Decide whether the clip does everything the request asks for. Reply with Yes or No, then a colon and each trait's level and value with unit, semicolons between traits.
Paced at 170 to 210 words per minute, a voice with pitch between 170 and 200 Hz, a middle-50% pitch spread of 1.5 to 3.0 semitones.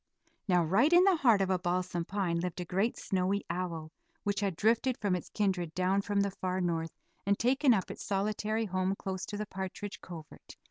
Yes: average, 200 wpm; high, 190 Hz; narrow, 2.5 semitones